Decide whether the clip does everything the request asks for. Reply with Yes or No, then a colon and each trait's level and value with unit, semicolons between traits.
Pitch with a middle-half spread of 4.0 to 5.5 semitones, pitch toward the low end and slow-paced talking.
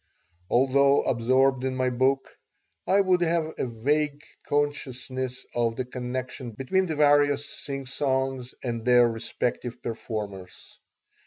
No: average, 2.8 semitones; low, 130 Hz; slow, 115 wpm